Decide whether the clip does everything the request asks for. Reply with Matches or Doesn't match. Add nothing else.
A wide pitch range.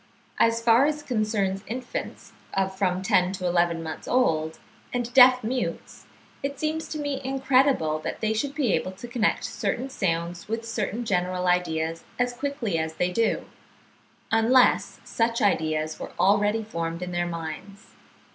Matches